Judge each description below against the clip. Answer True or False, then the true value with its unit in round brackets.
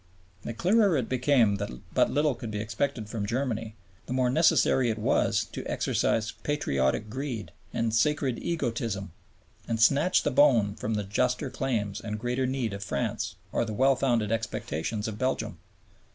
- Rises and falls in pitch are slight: False (3.9 semitones)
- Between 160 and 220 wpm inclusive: True (165 wpm)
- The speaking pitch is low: True (115 Hz)